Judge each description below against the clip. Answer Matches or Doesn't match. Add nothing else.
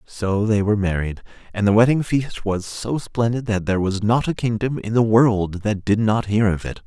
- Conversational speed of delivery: Doesn't match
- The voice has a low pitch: Matches